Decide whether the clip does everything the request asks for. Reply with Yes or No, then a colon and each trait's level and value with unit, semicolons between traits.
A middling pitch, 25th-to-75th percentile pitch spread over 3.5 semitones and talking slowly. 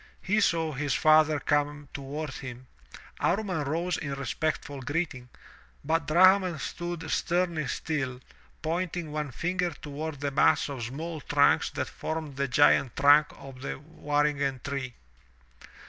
No: medium, 150 Hz; average, 2.9 semitones; slow, 130 wpm